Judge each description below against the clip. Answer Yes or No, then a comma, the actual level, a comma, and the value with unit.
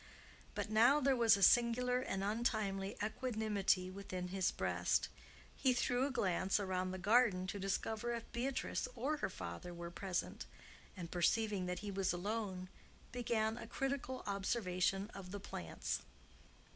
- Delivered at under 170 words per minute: Yes, average, 145 wpm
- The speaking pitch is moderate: No, high, 205 Hz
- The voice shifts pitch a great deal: No, average, 4.2 semitones